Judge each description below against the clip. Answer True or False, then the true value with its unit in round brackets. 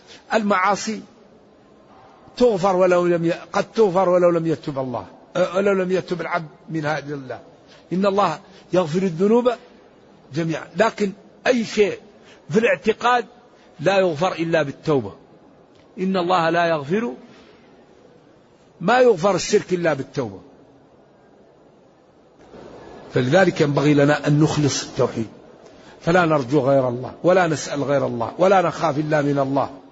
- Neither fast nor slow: True (120 wpm)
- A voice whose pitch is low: False (175 Hz)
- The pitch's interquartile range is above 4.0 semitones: True (5.2 semitones)